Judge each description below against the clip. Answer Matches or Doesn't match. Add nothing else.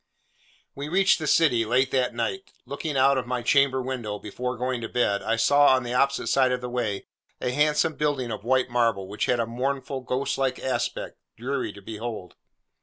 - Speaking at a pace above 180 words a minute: Matches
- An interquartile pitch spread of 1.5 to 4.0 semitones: Matches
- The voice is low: Matches